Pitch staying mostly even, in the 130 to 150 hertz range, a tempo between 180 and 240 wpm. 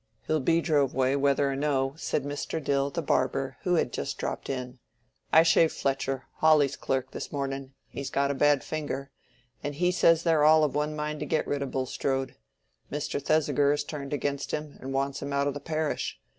Yes: narrow, 2.0 semitones; medium, 140 Hz; average, 195 wpm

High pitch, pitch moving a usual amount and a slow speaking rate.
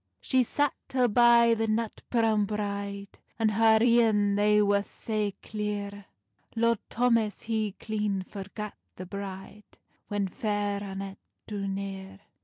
No: high, 210 Hz; narrow, 1.9 semitones; slow, 130 wpm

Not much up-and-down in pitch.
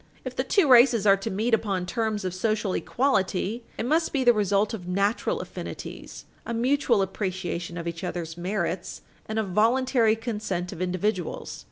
No: average, 4.3 semitones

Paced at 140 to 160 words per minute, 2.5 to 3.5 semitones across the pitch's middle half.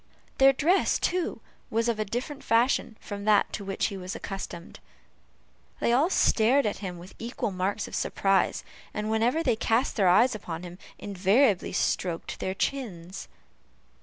No: average, 155 wpm; average, 4.3 semitones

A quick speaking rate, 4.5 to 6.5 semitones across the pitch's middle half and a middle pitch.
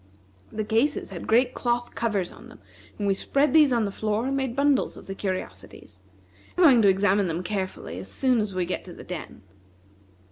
No: fast, 210 wpm; average, 4.9 semitones; high, 215 Hz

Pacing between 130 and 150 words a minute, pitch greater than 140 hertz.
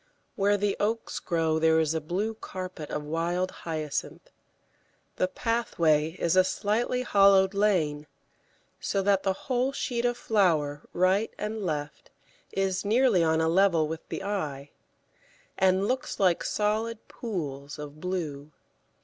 Yes: average, 140 wpm; medium, 185 Hz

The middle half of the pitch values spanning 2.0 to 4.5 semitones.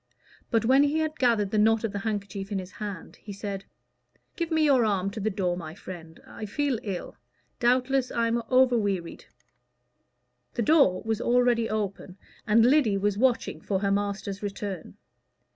Yes: average, 3.7 semitones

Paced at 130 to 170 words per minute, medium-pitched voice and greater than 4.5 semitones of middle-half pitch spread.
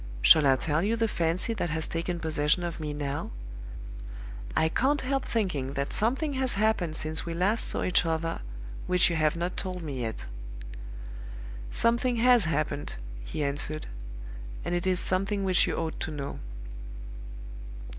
Yes: average, 160 wpm; medium, 170 Hz; average, 5.2 semitones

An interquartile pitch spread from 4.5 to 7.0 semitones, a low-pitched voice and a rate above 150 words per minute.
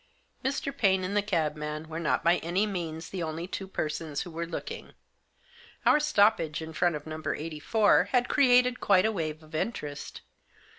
No: average, 4.8 semitones; medium, 170 Hz; average, 175 wpm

